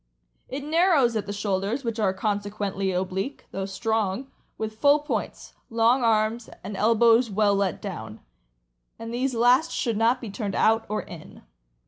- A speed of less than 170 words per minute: Yes, average, 155 wpm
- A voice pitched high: Yes, high, 220 Hz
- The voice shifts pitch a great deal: No, average, 3.2 semitones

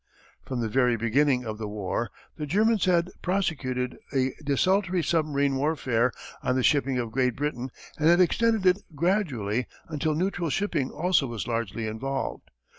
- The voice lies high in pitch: No, medium, 140 Hz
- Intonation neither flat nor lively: No, wide, 5.8 semitones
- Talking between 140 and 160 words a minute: Yes, average, 155 wpm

